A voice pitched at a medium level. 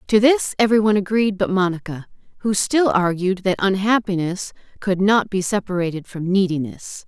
No: high, 195 Hz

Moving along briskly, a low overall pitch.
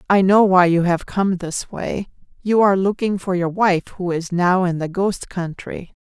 No: fast, 210 wpm; medium, 185 Hz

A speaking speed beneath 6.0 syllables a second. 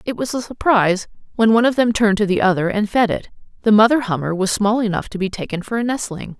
No: 6.5 syllables/s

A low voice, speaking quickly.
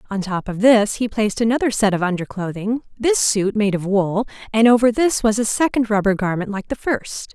No: high, 215 Hz; fast, 220 wpm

